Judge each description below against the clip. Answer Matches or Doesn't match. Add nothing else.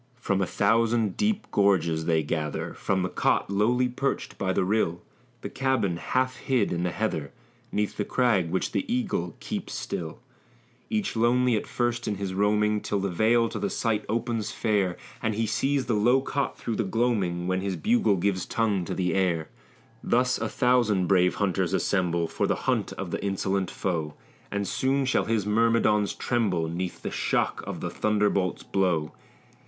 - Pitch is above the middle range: Doesn't match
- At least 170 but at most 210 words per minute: Matches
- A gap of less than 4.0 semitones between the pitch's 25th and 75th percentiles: Doesn't match